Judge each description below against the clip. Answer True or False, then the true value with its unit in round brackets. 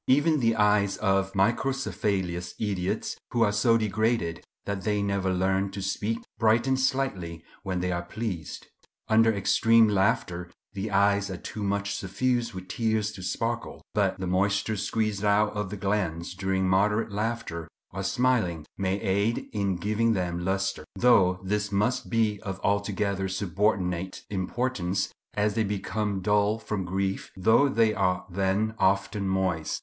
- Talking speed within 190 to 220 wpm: False (150 wpm)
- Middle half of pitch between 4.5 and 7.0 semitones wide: False (2.5 semitones)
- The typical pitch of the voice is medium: False (100 Hz)